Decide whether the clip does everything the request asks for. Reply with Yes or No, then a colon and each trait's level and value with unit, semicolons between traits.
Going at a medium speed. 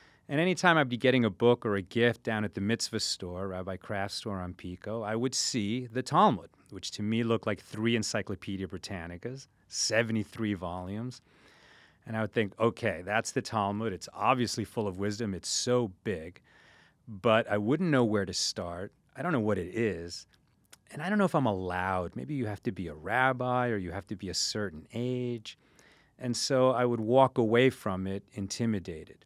Yes: average, 195 wpm